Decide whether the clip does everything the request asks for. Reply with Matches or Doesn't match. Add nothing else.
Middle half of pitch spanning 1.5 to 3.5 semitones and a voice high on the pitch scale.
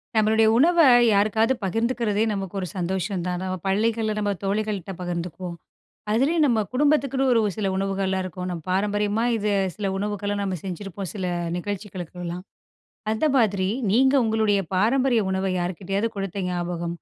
Matches